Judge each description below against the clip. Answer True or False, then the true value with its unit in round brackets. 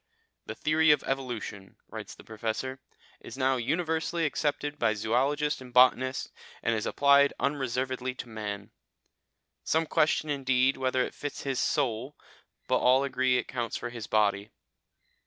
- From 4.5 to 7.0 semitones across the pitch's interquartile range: False (3.3 semitones)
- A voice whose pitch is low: True (130 Hz)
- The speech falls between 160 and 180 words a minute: False (150 wpm)